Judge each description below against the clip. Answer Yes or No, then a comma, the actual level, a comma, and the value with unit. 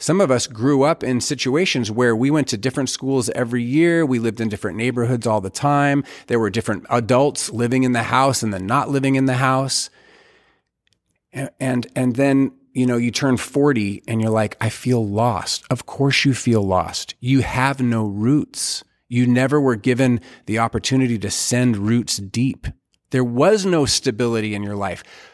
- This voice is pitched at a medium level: No, low, 125 Hz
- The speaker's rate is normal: Yes, average, 185 wpm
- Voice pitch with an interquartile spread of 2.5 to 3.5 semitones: Yes, average, 3.0 semitones